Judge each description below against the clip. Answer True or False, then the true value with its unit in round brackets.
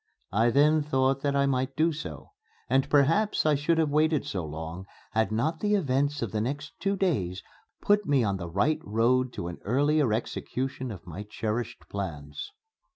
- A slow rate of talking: False (180 wpm)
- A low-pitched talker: True (130 Hz)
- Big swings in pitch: True (6.1 semitones)